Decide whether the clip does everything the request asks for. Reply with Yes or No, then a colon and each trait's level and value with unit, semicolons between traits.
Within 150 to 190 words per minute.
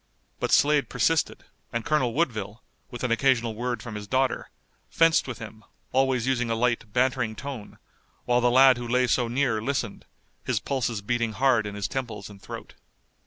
Yes: average, 175 wpm